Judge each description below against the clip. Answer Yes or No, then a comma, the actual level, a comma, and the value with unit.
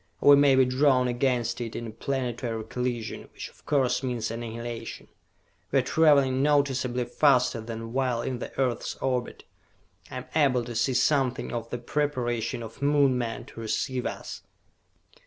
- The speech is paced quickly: No, average, 160 wpm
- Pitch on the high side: No, low, 125 Hz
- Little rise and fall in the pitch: Yes, narrow, 2.3 semitones